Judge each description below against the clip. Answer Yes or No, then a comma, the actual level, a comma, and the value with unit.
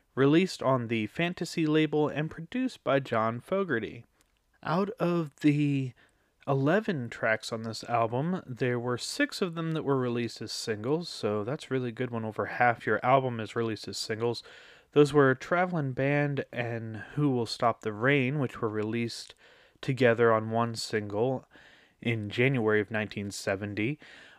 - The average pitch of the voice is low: Yes, low, 125 Hz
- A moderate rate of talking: Yes, average, 155 wpm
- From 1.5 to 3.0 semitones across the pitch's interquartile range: No, average, 4.7 semitones